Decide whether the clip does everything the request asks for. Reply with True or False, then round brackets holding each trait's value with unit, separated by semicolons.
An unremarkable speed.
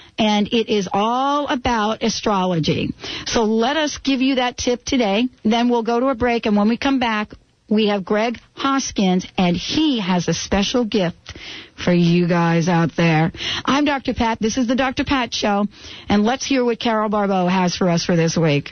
True (195 wpm)